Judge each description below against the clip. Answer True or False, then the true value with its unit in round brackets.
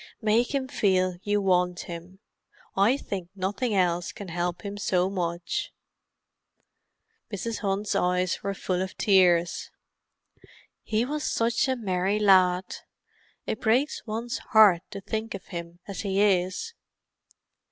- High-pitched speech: True (195 Hz)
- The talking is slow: True (130 wpm)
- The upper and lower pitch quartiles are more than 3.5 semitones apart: False (3.2 semitones)